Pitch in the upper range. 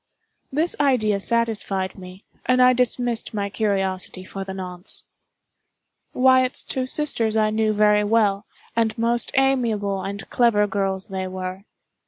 Yes: high, 215 Hz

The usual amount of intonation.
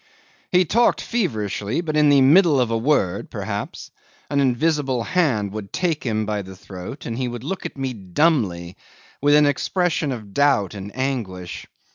No: wide, 6.4 semitones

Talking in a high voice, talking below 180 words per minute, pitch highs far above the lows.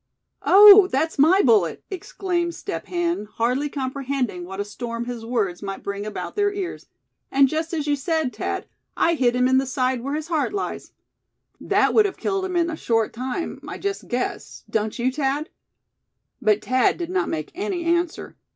No: very high, 275 Hz; average, 185 wpm; wide, 6.3 semitones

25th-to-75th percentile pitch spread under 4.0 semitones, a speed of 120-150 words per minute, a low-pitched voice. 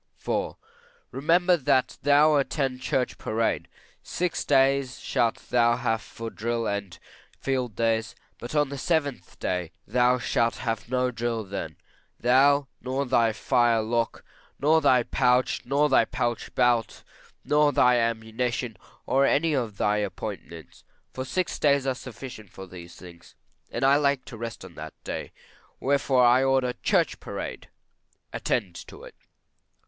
Yes: average, 3.2 semitones; average, 145 wpm; low, 125 Hz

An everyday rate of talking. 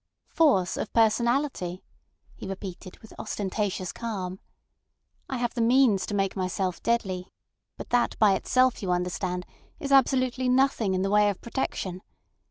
Yes: average, 145 wpm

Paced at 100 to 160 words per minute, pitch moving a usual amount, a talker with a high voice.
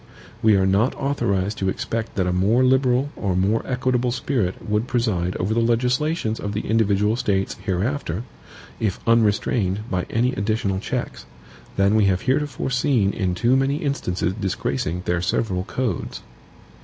No: average, 155 wpm; average, 4.6 semitones; low, 110 Hz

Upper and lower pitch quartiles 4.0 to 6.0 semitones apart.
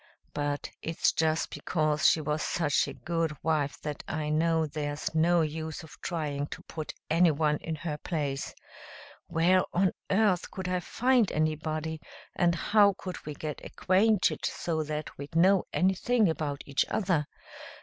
No: average, 2.9 semitones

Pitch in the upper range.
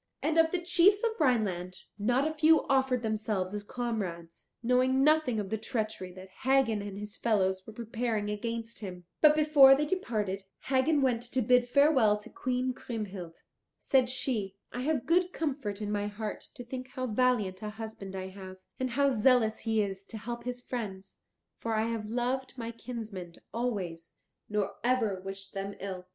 Yes: high, 230 Hz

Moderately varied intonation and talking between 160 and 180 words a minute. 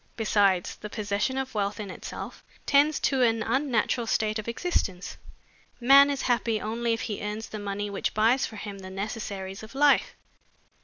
Yes: average, 3.3 semitones; average, 170 wpm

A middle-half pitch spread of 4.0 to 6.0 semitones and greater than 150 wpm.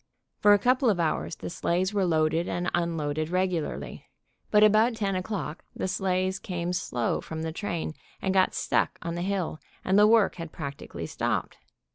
No: average, 3.2 semitones; average, 175 wpm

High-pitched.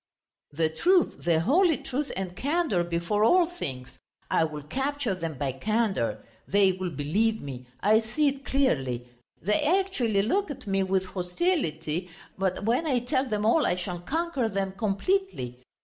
Yes: high, 200 Hz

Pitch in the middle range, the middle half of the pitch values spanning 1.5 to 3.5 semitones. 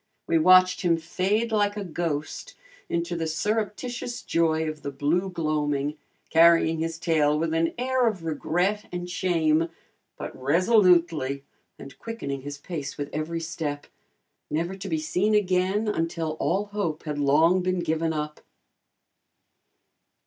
Yes: medium, 165 Hz; average, 3.2 semitones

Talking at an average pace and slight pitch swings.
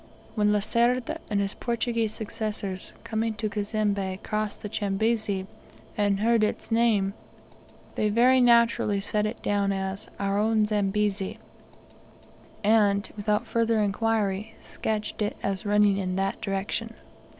No: slow, 130 wpm; narrow, 2.0 semitones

